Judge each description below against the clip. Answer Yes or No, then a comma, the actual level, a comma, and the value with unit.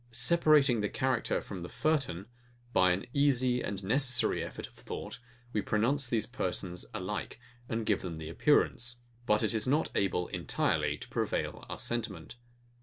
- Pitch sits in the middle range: No, low, 115 Hz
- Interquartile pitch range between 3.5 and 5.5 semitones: Yes, average, 5.2 semitones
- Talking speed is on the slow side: No, average, 155 wpm